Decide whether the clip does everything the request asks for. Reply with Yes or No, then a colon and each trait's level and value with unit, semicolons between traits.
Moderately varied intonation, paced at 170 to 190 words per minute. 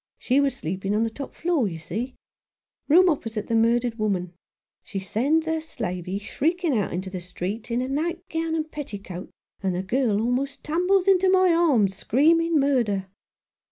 No: wide, 8.2 semitones; average, 175 wpm